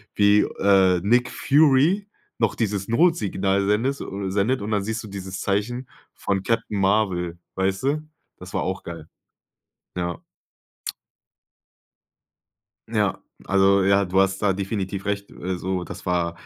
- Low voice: Yes, low, 100 Hz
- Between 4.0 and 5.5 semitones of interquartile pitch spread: No, average, 2.9 semitones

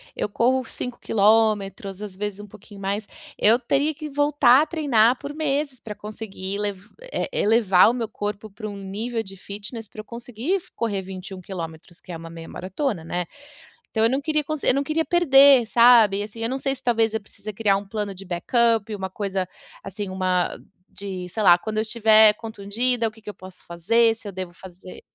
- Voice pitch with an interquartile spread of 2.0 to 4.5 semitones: Yes, average, 3.8 semitones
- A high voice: Yes, high, 215 Hz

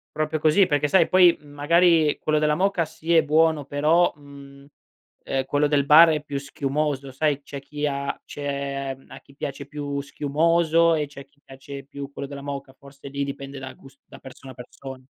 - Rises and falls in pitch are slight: Yes, narrow, 1.8 semitones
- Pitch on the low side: No, medium, 145 Hz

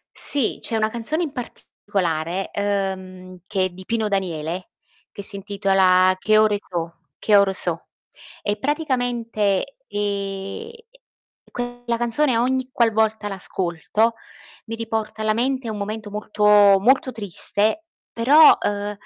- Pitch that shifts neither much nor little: Yes, average, 3.1 semitones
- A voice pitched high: Yes, high, 210 Hz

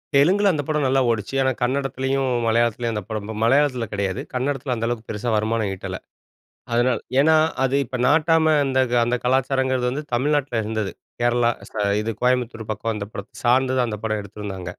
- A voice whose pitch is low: Yes, low, 120 Hz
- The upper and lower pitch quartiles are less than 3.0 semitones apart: No, average, 3.3 semitones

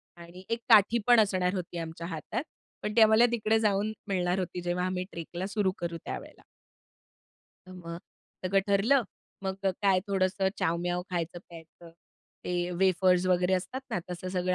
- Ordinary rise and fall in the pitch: No, narrow, 2.3 semitones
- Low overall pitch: No, medium, 185 Hz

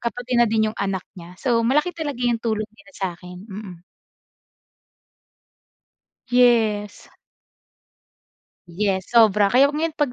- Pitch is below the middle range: No, high, 225 Hz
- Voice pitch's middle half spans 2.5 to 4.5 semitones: Yes, average, 3.9 semitones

